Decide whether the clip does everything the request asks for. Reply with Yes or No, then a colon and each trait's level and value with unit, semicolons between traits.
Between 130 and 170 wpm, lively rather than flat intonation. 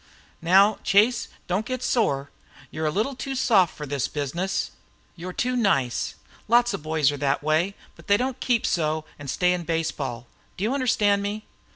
No: average, 190 wpm; wide, 6.4 semitones